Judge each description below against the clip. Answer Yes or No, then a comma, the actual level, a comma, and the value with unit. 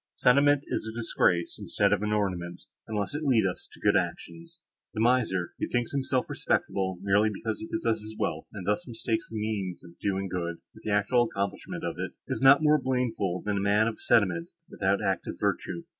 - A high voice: No, low, 105 Hz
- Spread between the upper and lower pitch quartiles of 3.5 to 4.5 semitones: Yes, average, 4.0 semitones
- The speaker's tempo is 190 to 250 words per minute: Yes, average, 195 wpm